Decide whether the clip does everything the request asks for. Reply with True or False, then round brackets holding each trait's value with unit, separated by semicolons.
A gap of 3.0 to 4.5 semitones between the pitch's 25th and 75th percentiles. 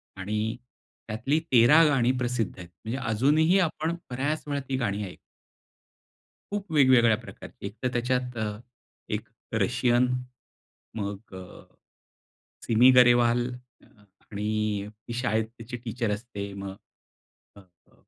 True (3.6 semitones)